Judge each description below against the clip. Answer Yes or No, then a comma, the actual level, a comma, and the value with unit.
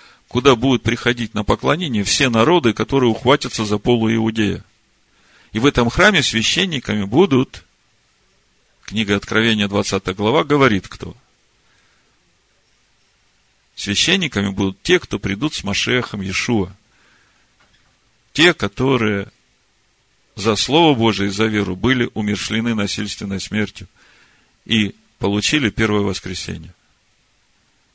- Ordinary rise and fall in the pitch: Yes, average, 3.3 semitones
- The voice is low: Yes, low, 110 Hz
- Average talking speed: No, slow, 105 wpm